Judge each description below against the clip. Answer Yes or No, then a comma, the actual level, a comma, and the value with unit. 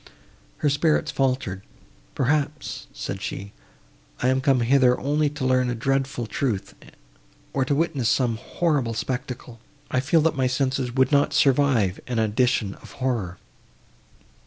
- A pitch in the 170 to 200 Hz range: No, low, 130 Hz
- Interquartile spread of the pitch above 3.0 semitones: No, average, 2.7 semitones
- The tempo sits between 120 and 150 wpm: Yes, average, 145 wpm